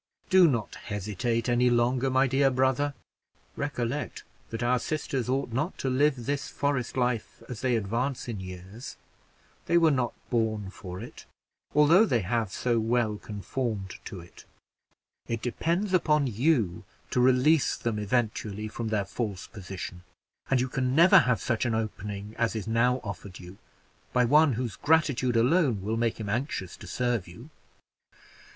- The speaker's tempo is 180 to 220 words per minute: No, average, 160 wpm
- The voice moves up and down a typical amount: Yes, average, 3.8 semitones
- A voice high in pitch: No, low, 120 Hz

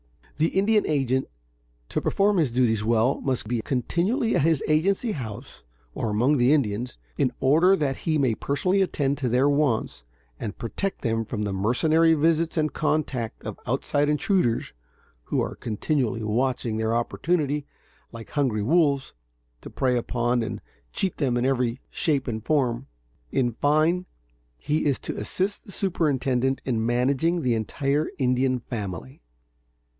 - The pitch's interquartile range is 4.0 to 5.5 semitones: Yes, average, 4.8 semitones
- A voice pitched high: No, low, 135 Hz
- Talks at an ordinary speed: Yes, average, 150 wpm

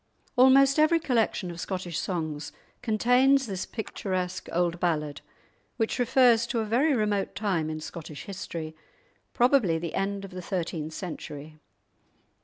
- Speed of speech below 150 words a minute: Yes, average, 140 wpm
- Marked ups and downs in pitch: Yes, wide, 6.2 semitones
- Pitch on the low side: No, high, 195 Hz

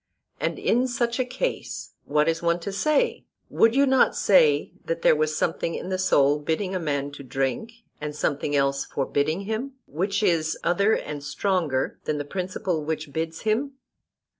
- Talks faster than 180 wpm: No, average, 175 wpm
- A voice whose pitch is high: No, medium, 165 Hz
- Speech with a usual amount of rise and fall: No, wide, 5.9 semitones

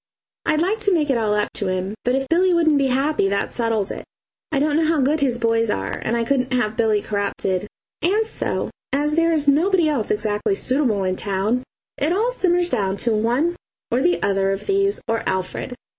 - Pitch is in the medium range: No, very high, 255 Hz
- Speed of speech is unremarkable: No, fast, 210 wpm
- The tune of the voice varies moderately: No, wide, 7.1 semitones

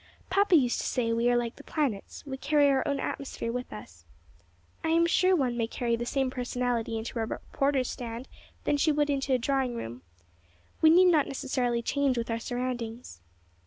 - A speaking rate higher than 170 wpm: Yes, average, 195 wpm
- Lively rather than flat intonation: No, average, 3.3 semitones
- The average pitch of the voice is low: No, very high, 255 Hz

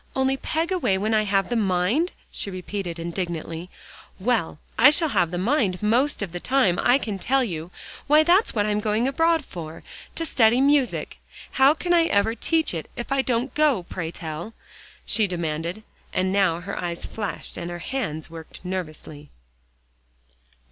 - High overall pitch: Yes, high, 205 Hz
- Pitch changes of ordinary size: No, wide, 7.3 semitones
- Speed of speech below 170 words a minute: No, average, 175 wpm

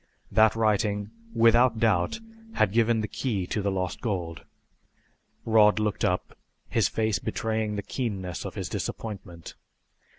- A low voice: Yes, low, 105 Hz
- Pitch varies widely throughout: No, average, 2.7 semitones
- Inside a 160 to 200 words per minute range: No, slow, 135 wpm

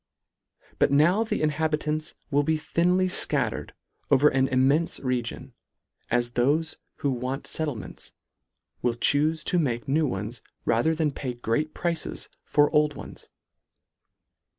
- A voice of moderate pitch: Yes, medium, 145 Hz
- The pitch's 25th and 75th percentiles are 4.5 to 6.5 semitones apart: No, average, 3.8 semitones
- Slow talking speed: Yes, slow, 130 wpm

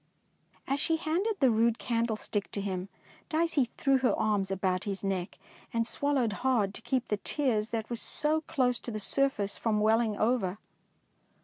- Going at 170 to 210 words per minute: Yes, average, 180 wpm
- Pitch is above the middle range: Yes, high, 230 Hz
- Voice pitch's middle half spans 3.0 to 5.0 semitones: Yes, average, 4.7 semitones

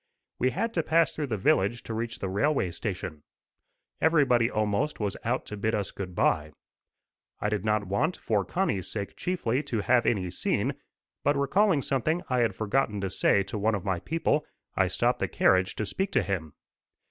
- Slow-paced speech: No, average, 190 wpm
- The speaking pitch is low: Yes, low, 110 Hz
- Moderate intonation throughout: No, wide, 6.0 semitones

